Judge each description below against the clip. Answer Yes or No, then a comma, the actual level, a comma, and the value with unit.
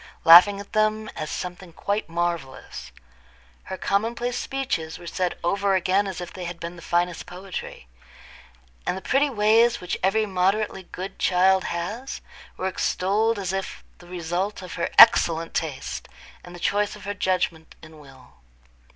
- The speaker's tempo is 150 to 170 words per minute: Yes, average, 160 wpm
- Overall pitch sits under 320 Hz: Yes, medium, 185 Hz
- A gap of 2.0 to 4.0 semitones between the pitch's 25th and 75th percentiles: Yes, average, 3.0 semitones